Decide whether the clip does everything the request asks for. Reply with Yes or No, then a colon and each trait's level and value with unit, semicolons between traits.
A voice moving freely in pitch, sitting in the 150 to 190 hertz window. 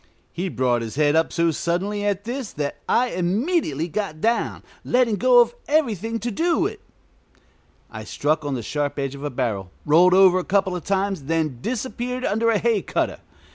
Yes: wide, 7.3 semitones; medium, 185 Hz